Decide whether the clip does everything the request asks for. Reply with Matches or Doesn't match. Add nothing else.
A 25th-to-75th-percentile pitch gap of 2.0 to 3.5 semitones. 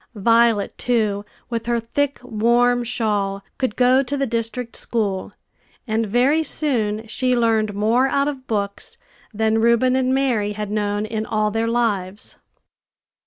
Matches